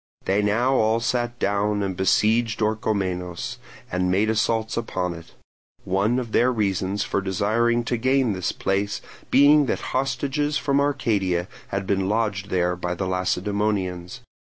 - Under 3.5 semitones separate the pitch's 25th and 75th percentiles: No, average, 4.0 semitones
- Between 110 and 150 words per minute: Yes, average, 145 wpm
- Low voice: Yes, low, 105 Hz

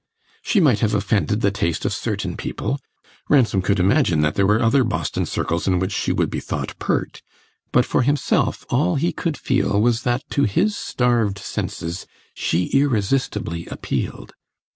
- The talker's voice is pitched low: Yes, low, 110 Hz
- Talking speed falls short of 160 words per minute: No, average, 165 wpm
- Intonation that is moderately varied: No, wide, 5.7 semitones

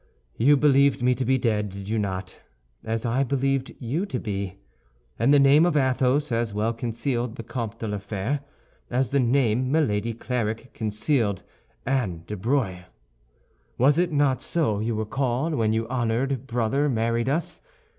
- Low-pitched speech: Yes, low, 120 Hz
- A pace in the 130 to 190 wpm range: Yes, average, 165 wpm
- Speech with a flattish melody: No, average, 3.9 semitones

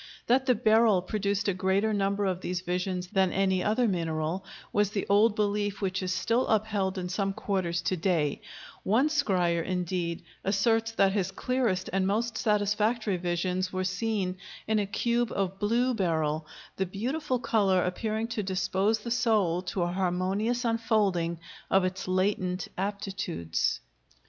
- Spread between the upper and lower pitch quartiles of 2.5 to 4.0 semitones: Yes, average, 3.0 semitones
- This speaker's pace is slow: No, average, 155 wpm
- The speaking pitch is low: No, high, 195 Hz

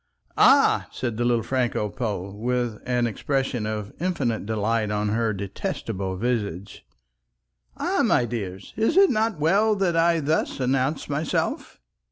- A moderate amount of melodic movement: No, wide, 5.9 semitones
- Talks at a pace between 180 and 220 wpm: No, average, 140 wpm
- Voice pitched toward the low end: Yes, low, 120 Hz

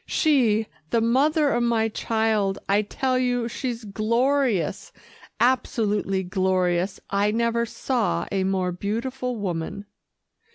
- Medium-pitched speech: No, high, 220 Hz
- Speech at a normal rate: No, slow, 115 wpm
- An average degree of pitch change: Yes, average, 4.0 semitones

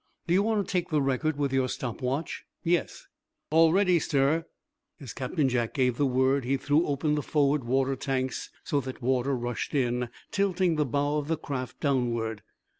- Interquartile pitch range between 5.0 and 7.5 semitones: No, average, 3.4 semitones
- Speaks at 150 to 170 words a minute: No, average, 190 wpm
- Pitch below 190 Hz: Yes, medium, 140 Hz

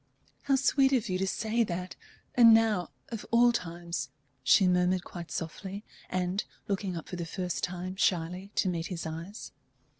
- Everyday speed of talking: Yes, average, 170 wpm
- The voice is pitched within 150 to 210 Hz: Yes, medium, 185 Hz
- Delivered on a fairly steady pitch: No, average, 3.7 semitones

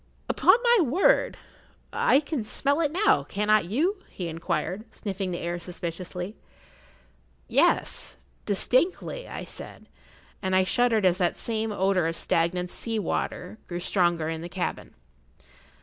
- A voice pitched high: Yes, high, 195 Hz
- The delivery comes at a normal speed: No, slow, 130 wpm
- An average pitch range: No, wide, 6.6 semitones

